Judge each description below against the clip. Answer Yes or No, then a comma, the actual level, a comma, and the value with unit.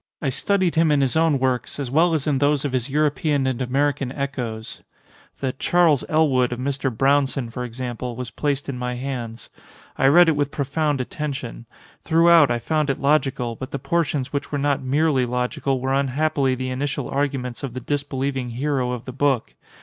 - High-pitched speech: No, low, 135 Hz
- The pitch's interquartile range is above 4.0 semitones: No, narrow, 2.5 semitones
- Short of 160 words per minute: No, average, 190 wpm